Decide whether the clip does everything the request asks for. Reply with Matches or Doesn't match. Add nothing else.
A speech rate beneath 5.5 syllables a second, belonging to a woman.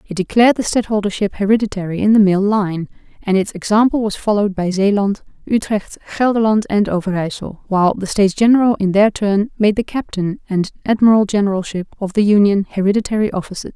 Doesn't match